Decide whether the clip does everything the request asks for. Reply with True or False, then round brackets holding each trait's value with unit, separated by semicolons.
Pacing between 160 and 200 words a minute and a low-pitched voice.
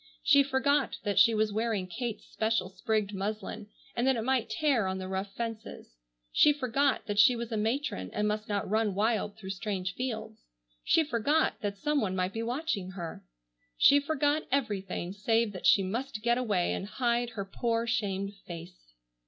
False (180 wpm; 220 Hz)